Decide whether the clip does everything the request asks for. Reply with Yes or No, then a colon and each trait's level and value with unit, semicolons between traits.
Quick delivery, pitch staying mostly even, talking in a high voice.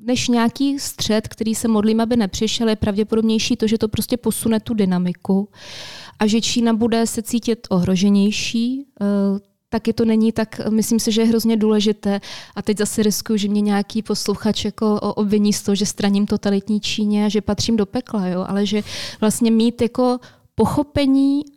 Yes: fast, 175 wpm; narrow, 1.9 semitones; high, 220 Hz